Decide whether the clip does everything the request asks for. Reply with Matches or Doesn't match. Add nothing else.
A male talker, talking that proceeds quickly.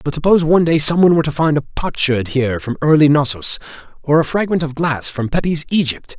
Matches